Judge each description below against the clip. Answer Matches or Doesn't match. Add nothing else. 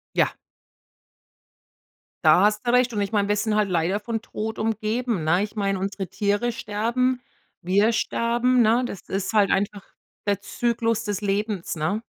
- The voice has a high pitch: Matches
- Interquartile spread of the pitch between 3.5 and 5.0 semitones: Doesn't match